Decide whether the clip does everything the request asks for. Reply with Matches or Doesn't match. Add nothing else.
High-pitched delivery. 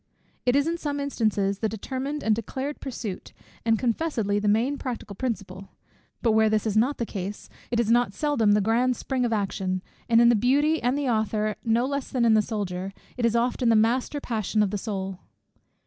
Matches